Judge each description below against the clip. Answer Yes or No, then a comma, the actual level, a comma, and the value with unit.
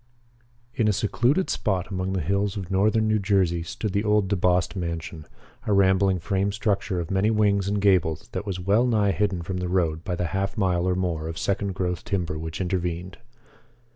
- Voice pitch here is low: Yes, very low, 95 Hz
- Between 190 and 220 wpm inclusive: Yes, average, 200 wpm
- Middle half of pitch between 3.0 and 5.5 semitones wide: No, narrow, 2.5 semitones